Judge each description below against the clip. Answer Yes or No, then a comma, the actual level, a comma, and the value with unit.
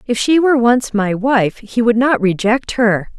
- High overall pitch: Yes, high, 230 Hz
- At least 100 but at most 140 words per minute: No, fast, 205 wpm